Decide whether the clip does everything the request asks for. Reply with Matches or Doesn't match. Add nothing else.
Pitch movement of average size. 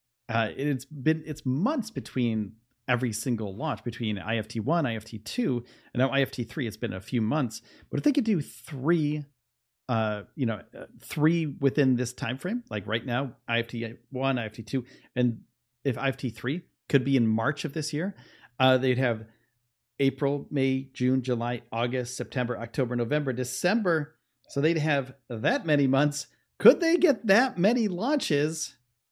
Matches